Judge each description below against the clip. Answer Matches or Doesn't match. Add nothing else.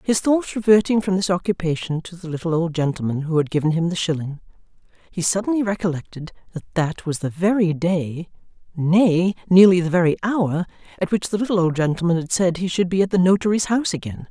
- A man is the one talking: Doesn't match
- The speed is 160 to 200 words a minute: Matches